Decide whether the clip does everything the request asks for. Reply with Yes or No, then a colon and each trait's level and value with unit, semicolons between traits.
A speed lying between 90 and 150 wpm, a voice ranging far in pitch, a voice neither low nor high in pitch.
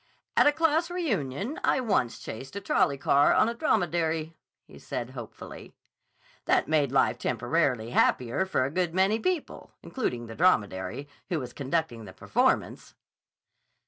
Yes: average, 145 wpm; wide, 8.1 semitones; medium, 155 Hz